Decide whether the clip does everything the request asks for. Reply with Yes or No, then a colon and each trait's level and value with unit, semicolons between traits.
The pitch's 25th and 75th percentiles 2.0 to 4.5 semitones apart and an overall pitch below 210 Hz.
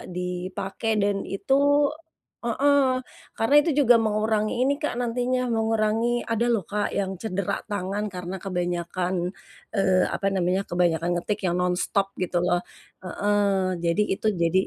Yes: average, 3.5 semitones; high, 200 Hz